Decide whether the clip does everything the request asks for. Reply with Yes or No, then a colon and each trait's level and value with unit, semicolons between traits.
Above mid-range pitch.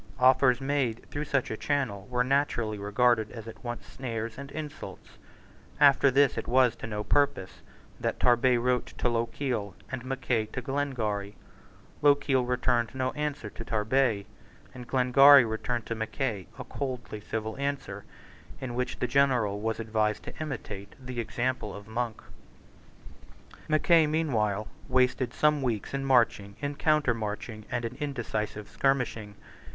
No: low, 125 Hz